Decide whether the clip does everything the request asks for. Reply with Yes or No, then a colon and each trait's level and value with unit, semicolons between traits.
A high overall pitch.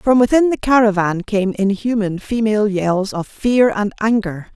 Yes: high, 210 Hz